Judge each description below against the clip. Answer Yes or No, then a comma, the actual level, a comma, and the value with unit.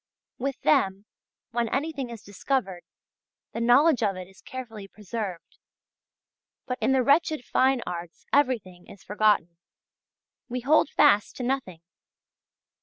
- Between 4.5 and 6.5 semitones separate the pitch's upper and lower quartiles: Yes, wide, 5.5 semitones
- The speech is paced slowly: Yes, slow, 125 wpm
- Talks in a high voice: Yes, high, 230 Hz